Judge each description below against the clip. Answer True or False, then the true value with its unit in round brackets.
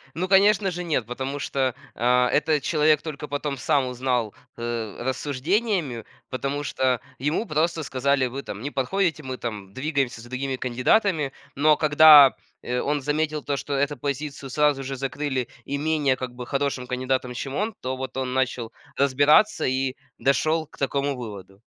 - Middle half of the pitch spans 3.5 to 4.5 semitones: False (2.8 semitones)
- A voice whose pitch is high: False (140 Hz)